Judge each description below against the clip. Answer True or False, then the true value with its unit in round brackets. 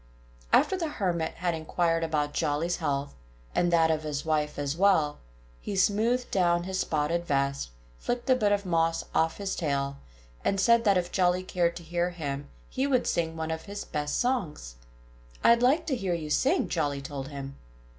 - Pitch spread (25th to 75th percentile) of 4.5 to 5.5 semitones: True (4.8 semitones)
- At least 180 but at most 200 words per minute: True (185 wpm)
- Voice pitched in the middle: True (170 Hz)